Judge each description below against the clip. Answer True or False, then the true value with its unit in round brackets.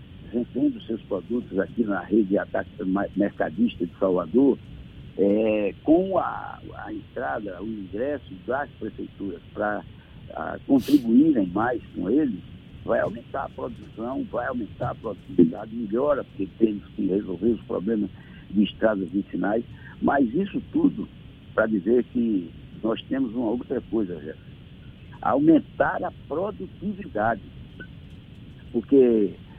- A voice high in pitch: False (120 Hz)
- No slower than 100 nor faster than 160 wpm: True (120 wpm)